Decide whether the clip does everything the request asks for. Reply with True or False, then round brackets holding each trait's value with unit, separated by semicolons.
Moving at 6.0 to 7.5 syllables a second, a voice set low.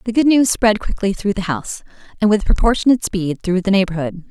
False (6.1 syllables/s; 200 Hz)